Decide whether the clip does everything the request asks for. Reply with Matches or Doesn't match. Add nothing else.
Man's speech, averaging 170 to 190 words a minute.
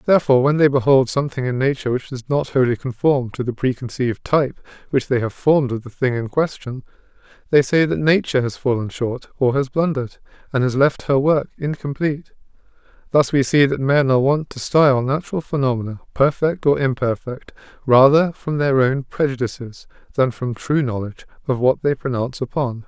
Matches